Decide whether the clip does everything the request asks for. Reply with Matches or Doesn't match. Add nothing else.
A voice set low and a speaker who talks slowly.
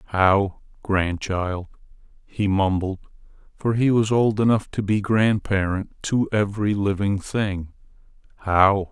Matches